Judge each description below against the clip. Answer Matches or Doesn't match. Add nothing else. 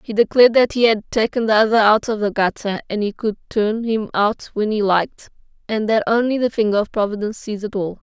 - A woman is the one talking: Matches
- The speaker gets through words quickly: Matches